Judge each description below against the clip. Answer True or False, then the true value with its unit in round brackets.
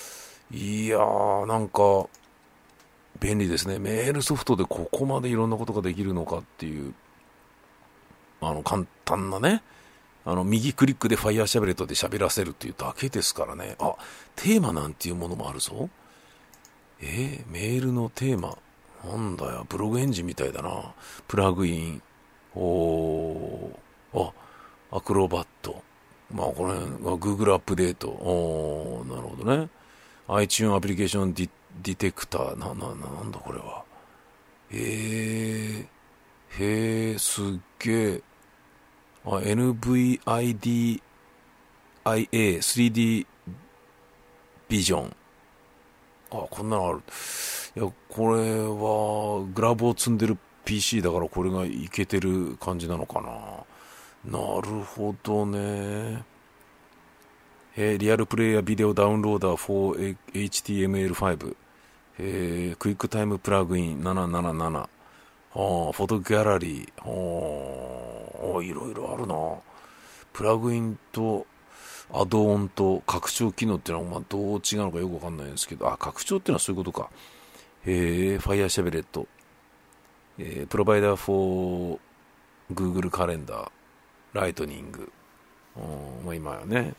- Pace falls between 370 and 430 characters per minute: False (285 characters per minute)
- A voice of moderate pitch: False (100 Hz)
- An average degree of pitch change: True (4.0 semitones)